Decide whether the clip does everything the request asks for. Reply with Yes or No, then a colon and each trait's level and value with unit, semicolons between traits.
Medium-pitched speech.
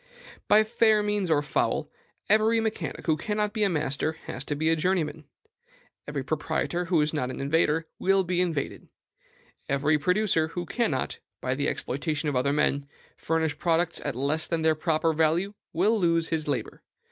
Yes: medium, 160 Hz